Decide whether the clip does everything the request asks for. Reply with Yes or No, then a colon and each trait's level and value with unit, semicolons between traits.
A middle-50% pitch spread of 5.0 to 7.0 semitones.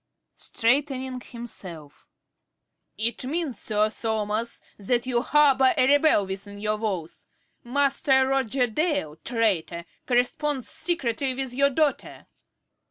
No: average, 4.2 semitones